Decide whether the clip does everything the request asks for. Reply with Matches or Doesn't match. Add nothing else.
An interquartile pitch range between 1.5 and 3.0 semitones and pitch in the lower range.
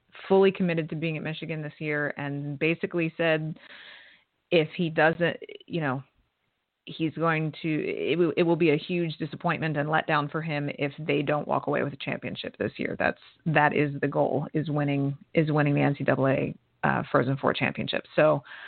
Doesn't match